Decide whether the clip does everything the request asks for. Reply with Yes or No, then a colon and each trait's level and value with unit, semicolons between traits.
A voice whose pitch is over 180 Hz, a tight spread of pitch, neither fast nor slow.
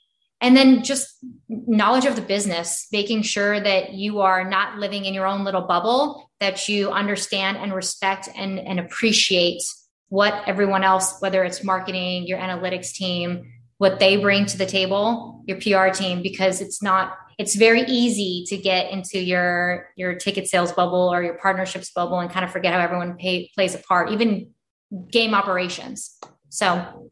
Yes: high, 190 Hz; narrow, 1.8 semitones; average, 170 wpm